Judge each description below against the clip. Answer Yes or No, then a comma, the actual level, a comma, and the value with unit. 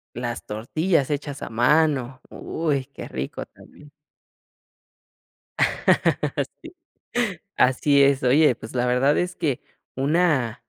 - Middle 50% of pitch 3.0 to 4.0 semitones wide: Yes, average, 3.4 semitones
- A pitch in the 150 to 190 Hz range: No, low, 135 Hz